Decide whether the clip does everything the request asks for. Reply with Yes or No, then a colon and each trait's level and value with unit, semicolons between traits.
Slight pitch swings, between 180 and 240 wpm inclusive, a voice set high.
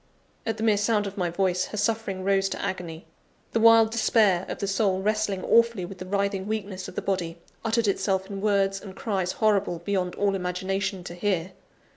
Yes: narrow, 2.2 semitones; average, 195 wpm; high, 195 Hz